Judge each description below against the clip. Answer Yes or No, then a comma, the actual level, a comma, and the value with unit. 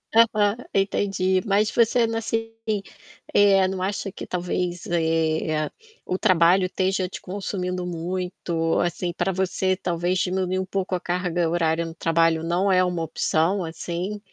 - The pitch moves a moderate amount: No, narrow, 2.2 semitones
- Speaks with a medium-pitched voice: Yes, medium, 180 Hz